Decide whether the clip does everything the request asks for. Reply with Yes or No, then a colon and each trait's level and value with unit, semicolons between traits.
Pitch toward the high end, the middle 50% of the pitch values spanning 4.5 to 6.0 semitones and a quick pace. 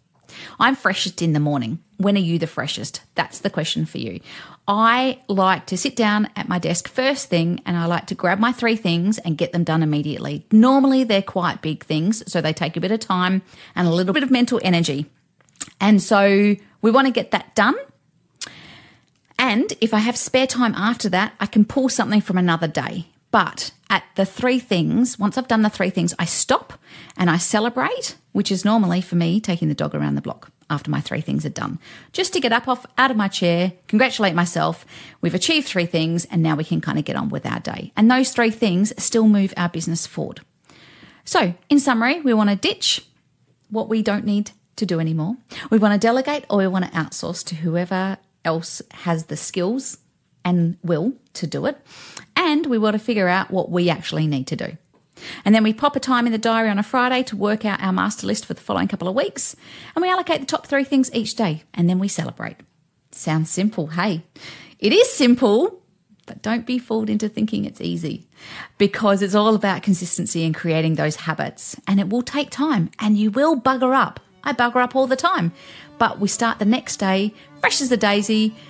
Yes: high, 205 Hz; average, 5.3 semitones; fast, 210 wpm